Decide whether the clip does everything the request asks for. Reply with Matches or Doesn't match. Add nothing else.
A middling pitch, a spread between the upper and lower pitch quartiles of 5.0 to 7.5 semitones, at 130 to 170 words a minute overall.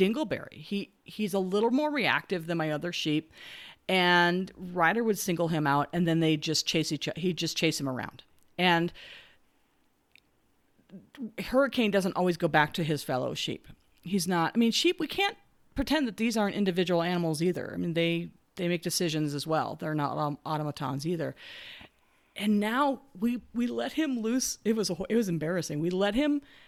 Doesn't match